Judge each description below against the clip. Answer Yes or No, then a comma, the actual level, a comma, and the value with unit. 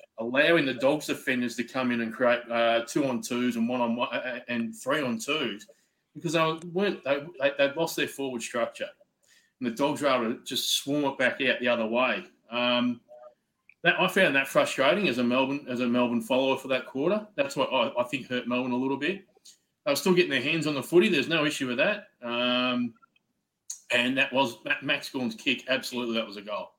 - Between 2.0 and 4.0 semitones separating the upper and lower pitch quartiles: No, average, 5.3 semitones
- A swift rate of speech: Yes, fast, 215 wpm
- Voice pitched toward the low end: Yes, low, 130 Hz